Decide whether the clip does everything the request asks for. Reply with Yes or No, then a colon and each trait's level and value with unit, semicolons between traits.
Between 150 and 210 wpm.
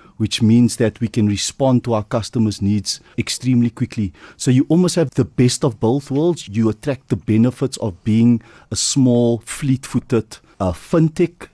Yes: average, 170 wpm